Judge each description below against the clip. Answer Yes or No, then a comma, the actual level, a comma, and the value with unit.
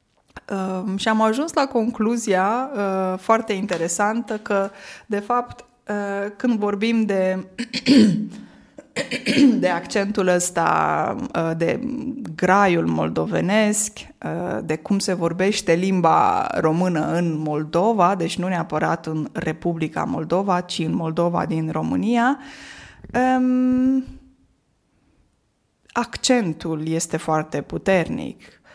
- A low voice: No, high, 200 Hz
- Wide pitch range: Yes, wide, 5.9 semitones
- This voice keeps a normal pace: No, slow, 100 wpm